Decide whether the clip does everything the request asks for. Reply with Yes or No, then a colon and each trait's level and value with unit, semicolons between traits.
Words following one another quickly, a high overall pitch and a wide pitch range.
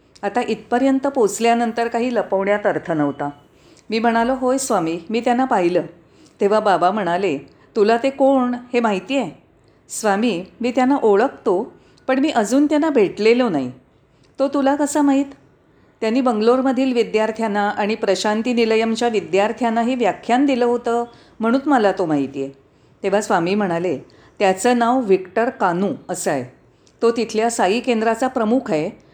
No: fast, 140 wpm; high, 230 Hz; average, 4.1 semitones